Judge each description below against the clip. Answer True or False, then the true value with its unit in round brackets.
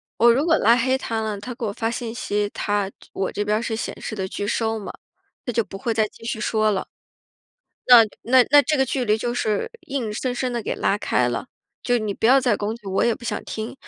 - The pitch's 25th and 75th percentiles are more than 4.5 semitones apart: False (2.8 semitones)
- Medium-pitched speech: False (225 Hz)